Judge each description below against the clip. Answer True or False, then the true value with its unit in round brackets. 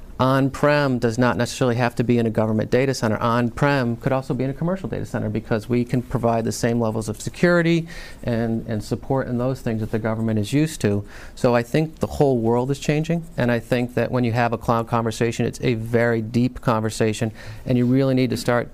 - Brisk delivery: True (235 wpm)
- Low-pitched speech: True (120 Hz)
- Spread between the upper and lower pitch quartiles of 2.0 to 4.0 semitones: True (2.4 semitones)